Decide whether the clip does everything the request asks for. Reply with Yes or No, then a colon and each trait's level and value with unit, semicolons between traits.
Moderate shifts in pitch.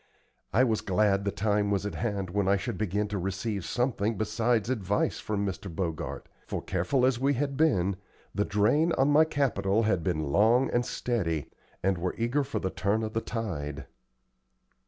Yes: average, 3.9 semitones